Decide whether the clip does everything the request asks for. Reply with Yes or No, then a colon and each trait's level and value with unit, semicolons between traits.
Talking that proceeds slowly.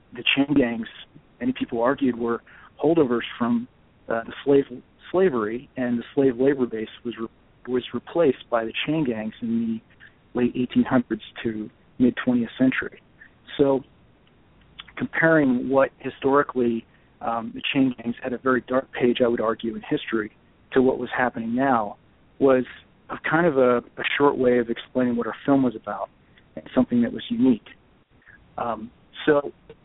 No: average, 160 wpm